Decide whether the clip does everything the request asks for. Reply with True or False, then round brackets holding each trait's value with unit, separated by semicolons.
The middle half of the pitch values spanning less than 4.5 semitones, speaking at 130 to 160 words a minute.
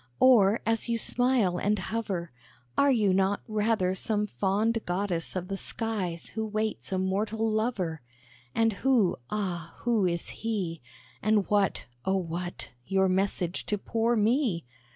True (3.3 semitones; 145 wpm)